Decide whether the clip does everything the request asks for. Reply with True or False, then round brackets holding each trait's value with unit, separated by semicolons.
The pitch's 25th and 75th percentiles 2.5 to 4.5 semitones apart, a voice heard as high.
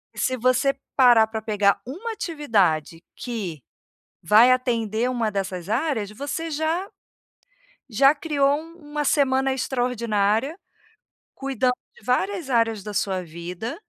False (4.9 semitones; 245 Hz)